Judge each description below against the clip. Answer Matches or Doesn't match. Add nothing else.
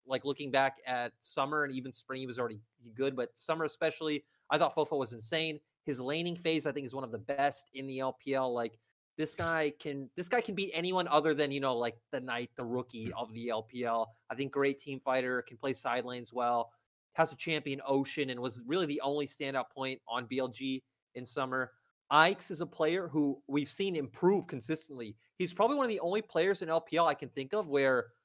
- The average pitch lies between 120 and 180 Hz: Matches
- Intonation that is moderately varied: Matches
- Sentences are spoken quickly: Matches